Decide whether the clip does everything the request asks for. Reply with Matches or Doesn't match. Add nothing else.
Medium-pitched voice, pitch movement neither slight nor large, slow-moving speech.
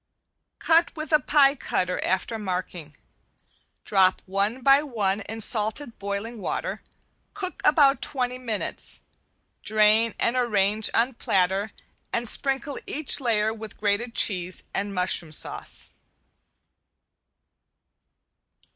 Doesn't match